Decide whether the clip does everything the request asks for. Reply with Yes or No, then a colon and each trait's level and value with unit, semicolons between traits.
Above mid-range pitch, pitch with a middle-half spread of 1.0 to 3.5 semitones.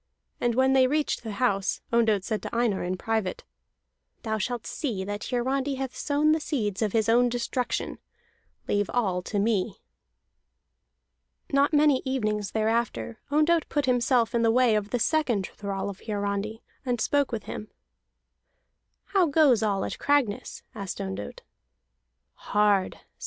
No: high, 230 Hz; average, 4.3 semitones